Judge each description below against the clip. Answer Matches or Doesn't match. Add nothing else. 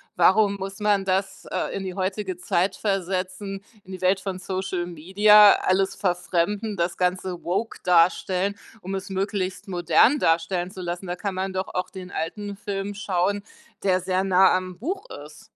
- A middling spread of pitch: Doesn't match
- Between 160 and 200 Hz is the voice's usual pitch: Matches